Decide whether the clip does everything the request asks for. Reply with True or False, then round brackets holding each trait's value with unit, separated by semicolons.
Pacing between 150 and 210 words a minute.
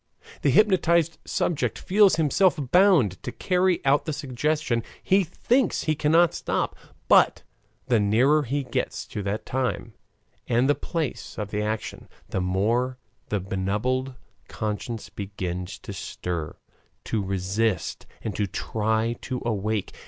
False (135 wpm)